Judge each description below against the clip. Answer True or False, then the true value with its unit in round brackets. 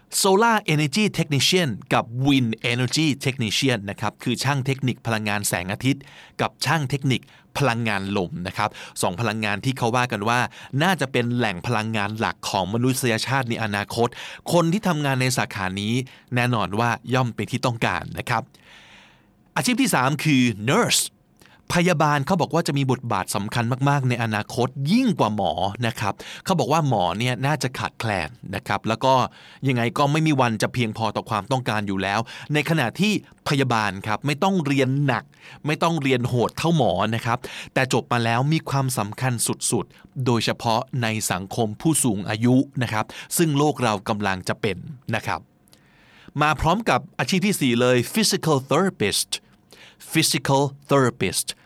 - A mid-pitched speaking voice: False (125 Hz)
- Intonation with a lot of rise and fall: False (4.4 semitones)